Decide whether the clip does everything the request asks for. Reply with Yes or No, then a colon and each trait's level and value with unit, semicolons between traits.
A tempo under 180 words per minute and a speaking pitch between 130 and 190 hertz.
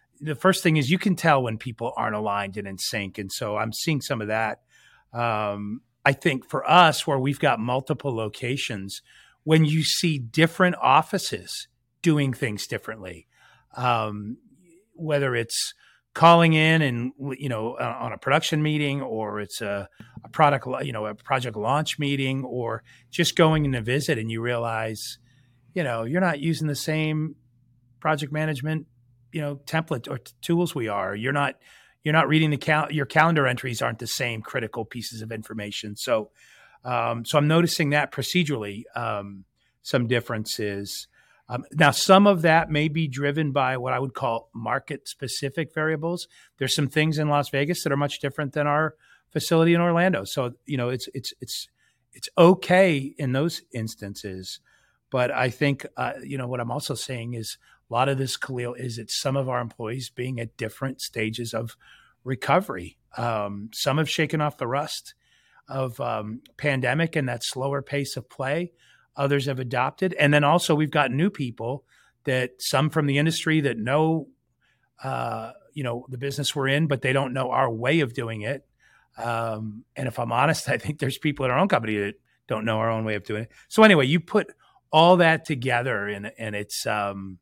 No: average, 185 wpm; low, 135 Hz